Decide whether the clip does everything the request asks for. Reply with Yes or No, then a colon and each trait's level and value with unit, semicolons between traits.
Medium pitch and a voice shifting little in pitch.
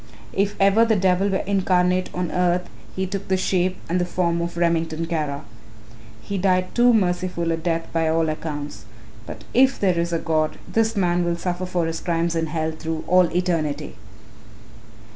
Yes: medium, 175 Hz; narrow, 2.2 semitones